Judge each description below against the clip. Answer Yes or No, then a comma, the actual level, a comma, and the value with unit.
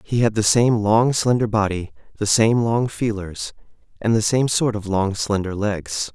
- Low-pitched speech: Yes, low, 110 Hz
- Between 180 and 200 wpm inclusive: Yes, average, 185 wpm